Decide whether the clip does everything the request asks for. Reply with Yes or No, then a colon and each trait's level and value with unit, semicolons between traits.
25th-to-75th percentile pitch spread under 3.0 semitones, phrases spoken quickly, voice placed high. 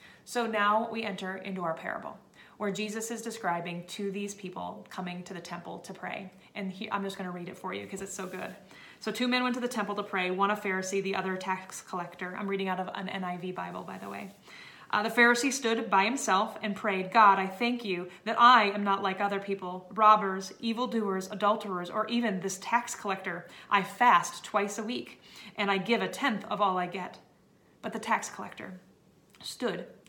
Yes: narrow, 2.6 semitones; fast, 215 wpm; high, 200 Hz